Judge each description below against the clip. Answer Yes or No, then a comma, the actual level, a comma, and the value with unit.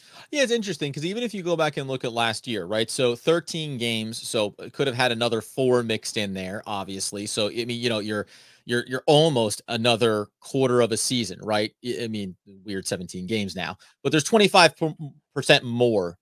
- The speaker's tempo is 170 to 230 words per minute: Yes, average, 200 wpm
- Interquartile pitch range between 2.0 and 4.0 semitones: No, wide, 5.4 semitones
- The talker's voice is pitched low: Yes, low, 120 Hz